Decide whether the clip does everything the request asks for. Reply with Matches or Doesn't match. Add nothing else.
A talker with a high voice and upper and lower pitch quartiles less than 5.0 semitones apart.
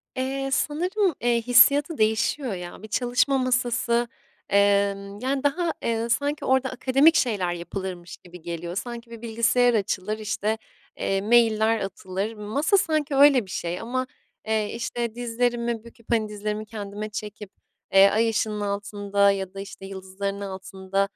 Matches